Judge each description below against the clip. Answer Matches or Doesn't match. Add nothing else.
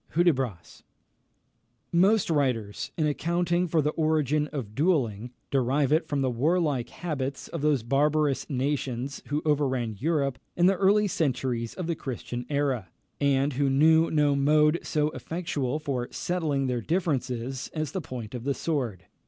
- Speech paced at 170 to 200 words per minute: Doesn't match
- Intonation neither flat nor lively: Matches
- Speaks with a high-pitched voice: Doesn't match